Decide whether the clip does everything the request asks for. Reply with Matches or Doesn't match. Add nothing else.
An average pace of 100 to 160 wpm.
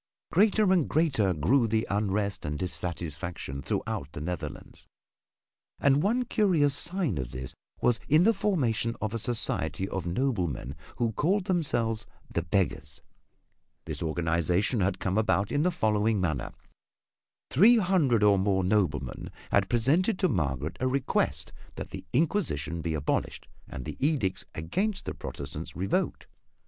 Matches